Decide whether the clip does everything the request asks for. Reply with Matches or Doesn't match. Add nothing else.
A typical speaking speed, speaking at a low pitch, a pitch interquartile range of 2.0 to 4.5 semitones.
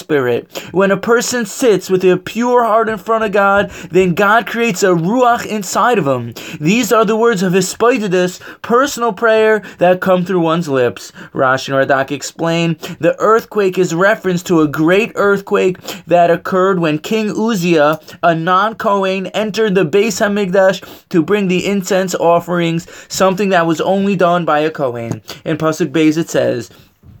Doesn't match